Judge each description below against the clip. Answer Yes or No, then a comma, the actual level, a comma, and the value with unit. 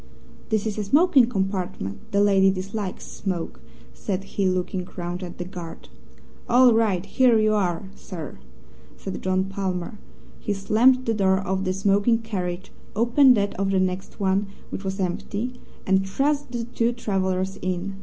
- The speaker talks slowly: No, average, 160 wpm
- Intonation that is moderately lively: Yes, average, 3.0 semitones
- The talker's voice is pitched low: No, high, 195 Hz